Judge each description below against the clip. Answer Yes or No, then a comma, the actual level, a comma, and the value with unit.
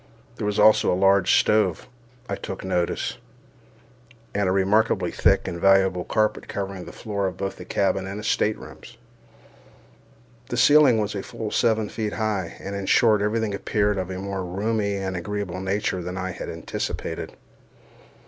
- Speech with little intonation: Yes, narrow, 2.1 semitones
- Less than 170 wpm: Yes, average, 160 wpm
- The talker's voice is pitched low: Yes, low, 100 Hz